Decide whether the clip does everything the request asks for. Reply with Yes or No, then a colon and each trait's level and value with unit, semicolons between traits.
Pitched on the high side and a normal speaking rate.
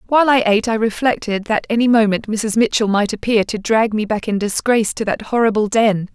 No: high, 220 Hz; fast, 215 wpm